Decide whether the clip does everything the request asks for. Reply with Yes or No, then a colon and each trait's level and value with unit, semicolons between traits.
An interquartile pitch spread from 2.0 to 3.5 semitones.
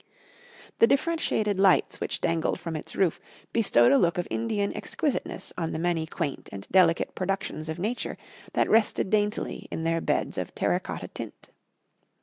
No: average, 4.4 semitones